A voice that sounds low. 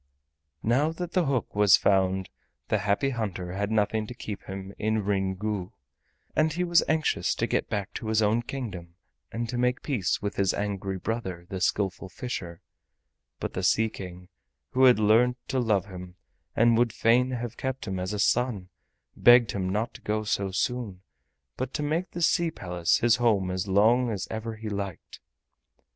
Yes: low, 110 Hz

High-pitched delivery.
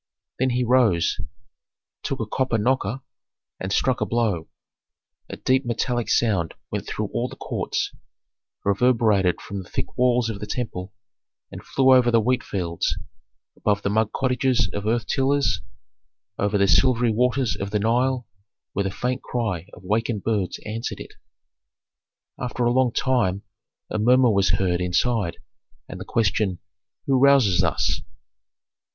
No: low, 115 Hz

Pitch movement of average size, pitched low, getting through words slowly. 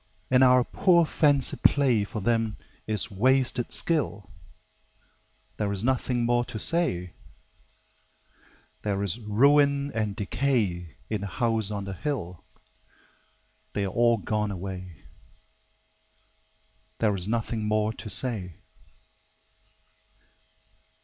Yes: average, 4.2 semitones; low, 110 Hz; slow, 110 wpm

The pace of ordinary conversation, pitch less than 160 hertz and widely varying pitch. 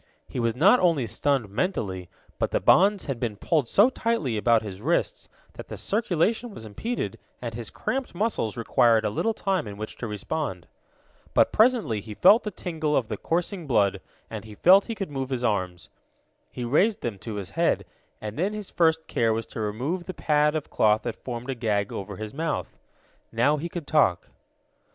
Yes: average, 195 wpm; low, 135 Hz; wide, 8.8 semitones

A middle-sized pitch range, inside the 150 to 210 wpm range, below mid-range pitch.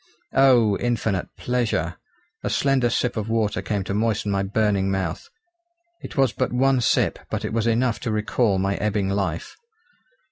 Yes: average, 3.6 semitones; average, 165 wpm; low, 110 Hz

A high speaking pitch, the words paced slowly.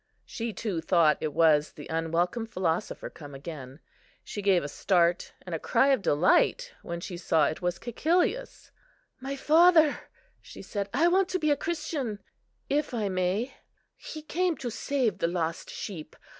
No: high, 200 Hz; average, 165 wpm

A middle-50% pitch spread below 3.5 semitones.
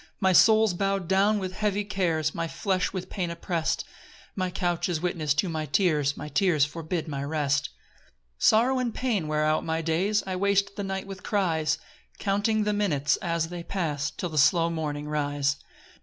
No: average, 4.2 semitones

